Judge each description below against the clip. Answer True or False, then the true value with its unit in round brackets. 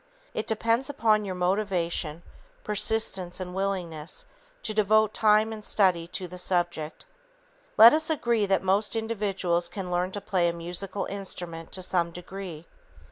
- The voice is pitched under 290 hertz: True (190 Hz)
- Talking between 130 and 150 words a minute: True (145 wpm)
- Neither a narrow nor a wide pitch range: True (3.4 semitones)